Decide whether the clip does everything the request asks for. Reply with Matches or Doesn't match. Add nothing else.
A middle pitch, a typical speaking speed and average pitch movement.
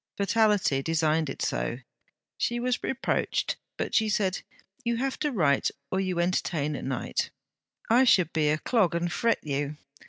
Doesn't match